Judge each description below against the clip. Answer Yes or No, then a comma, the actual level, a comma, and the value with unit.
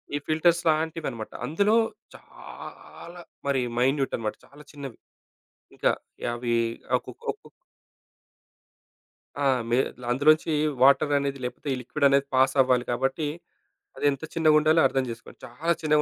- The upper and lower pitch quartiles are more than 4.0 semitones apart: No, average, 3.4 semitones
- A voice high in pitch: No, medium, 140 Hz